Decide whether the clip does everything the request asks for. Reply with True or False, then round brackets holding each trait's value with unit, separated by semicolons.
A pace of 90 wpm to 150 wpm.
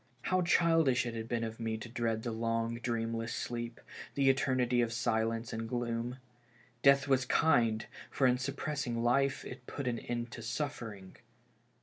False (160 wpm)